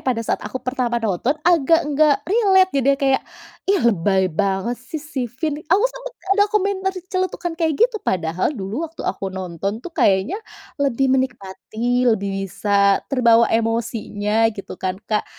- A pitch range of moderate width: No, wide, 8.0 semitones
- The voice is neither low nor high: No, high, 245 Hz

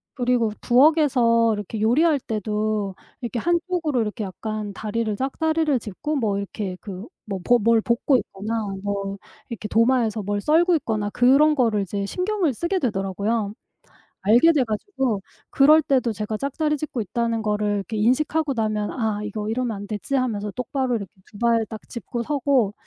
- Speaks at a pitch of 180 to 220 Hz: No, high, 230 Hz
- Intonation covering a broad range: No, average, 4.4 semitones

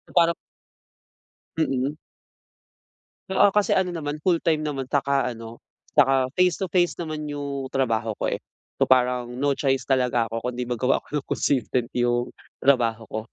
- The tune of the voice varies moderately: Yes, average, 3.6 semitones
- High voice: No, low, 135 Hz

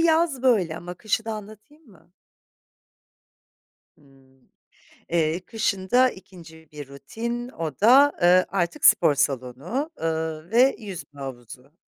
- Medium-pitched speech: Yes, medium, 180 Hz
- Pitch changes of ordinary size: No, wide, 7.0 semitones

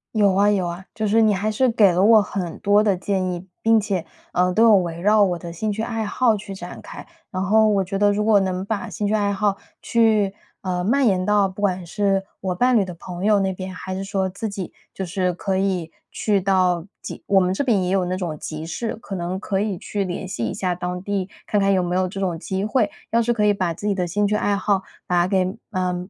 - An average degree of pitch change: No, narrow, 2.3 semitones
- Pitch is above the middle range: Yes, high, 195 Hz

